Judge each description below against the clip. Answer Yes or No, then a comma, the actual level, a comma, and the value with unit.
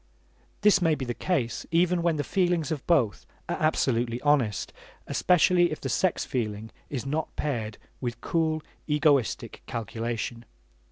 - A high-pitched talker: No, medium, 145 Hz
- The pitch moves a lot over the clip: Yes, wide, 5.9 semitones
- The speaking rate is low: No, average, 145 wpm